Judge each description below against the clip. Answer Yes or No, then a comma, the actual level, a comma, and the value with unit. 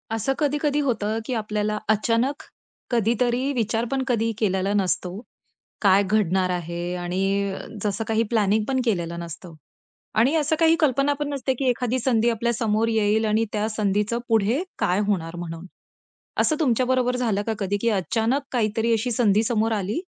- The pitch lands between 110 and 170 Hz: No, high, 220 Hz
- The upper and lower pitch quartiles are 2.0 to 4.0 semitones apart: Yes, average, 3.6 semitones